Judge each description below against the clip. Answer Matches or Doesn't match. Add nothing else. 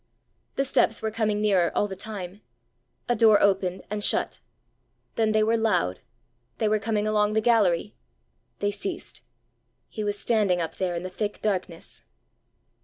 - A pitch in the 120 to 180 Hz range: Doesn't match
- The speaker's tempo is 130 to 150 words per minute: Doesn't match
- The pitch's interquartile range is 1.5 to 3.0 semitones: Matches